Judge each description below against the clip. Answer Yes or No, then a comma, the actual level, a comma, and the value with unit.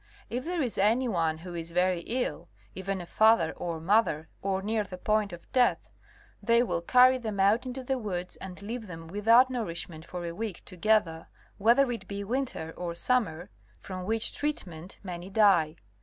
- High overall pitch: Yes, high, 200 Hz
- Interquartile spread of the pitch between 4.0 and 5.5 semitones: Yes, average, 5.0 semitones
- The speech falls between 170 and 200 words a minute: Yes, average, 180 wpm